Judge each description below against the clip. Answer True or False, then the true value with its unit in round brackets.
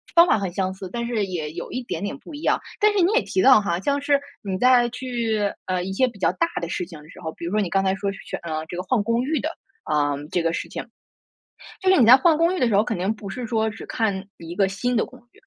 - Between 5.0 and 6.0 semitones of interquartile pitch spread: True (5.4 semitones)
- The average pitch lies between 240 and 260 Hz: False (215 Hz)